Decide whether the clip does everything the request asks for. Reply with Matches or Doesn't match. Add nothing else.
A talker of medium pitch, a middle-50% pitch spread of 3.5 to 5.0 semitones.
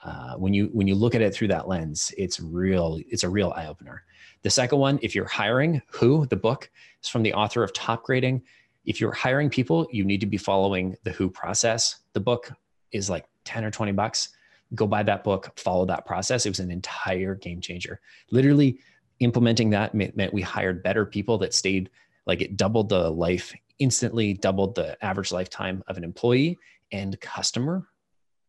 Doesn't match